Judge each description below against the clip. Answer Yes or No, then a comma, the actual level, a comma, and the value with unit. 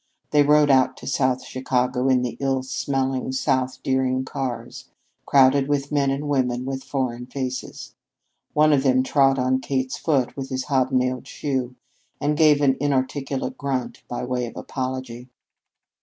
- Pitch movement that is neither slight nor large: No, narrow, 1.4 semitones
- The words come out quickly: No, average, 155 wpm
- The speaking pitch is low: Yes, low, 130 Hz